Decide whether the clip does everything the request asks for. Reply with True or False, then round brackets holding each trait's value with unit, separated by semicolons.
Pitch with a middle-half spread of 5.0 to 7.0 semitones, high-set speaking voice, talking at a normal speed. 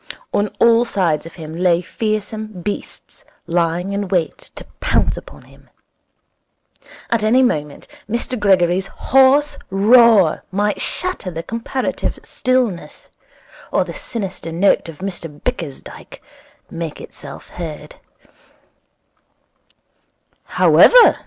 False (5.3 semitones; 195 Hz; 105 wpm)